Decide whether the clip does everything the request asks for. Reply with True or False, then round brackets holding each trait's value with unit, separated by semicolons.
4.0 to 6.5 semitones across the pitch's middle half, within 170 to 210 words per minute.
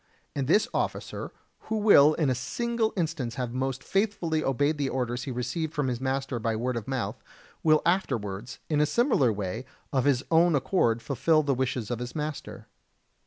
True (4.4 semitones; 180 wpm)